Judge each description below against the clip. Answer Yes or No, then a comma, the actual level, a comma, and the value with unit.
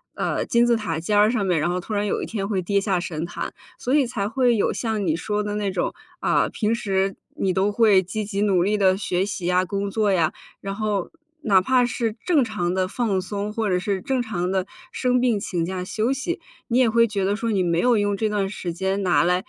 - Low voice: No, high, 200 Hz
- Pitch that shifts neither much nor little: Yes, average, 3.1 semitones